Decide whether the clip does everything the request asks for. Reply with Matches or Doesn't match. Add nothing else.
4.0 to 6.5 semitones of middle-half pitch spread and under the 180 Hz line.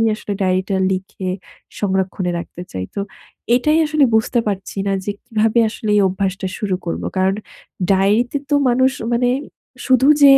Doesn't match